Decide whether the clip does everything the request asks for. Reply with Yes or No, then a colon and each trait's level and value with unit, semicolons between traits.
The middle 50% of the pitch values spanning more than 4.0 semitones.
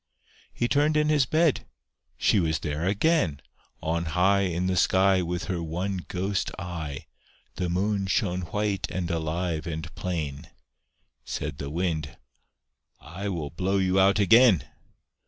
No: average, 3.1 semitones